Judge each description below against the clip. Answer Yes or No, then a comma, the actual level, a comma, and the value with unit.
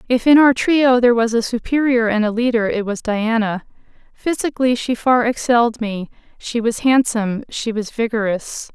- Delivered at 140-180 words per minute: Yes, average, 170 wpm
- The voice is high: Yes, high, 235 Hz